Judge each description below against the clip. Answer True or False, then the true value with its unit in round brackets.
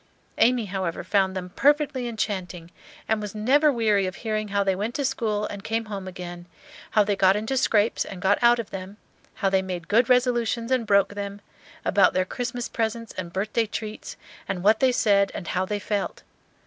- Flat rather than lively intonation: False (3.3 semitones)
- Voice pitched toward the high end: True (210 Hz)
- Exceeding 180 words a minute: True (195 wpm)